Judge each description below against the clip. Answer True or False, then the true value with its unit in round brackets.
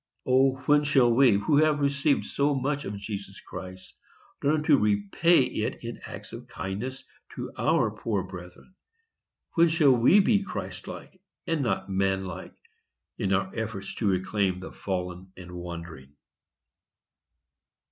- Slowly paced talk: False (145 wpm)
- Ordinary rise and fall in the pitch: False (7.0 semitones)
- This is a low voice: True (110 Hz)